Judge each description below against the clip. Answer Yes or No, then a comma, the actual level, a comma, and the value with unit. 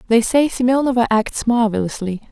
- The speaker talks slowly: Yes, slow, 130 wpm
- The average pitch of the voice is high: Yes, high, 235 Hz